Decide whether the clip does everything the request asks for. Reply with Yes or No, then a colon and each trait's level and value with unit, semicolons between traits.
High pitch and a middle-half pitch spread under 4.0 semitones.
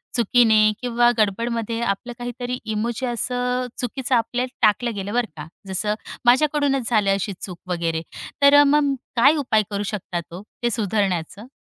Yes: high, 235 Hz; average, 3.4 semitones